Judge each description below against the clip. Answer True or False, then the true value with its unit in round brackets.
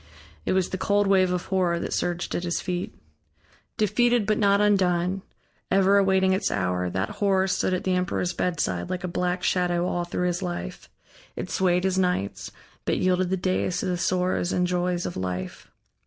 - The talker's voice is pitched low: False (180 Hz)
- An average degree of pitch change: False (1.4 semitones)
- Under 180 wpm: False (185 wpm)